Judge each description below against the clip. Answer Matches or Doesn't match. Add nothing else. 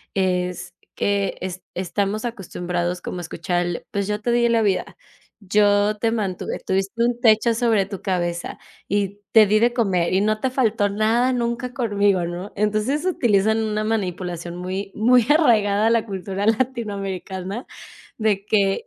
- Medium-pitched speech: Doesn't match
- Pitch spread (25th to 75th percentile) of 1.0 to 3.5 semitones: Matches